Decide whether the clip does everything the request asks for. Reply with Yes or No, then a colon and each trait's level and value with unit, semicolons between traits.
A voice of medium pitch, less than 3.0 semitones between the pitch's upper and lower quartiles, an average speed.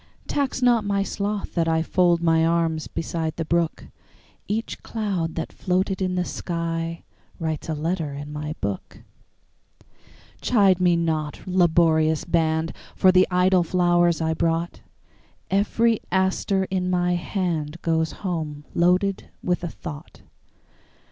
No: medium, 170 Hz; narrow, 2.5 semitones; slow, 115 wpm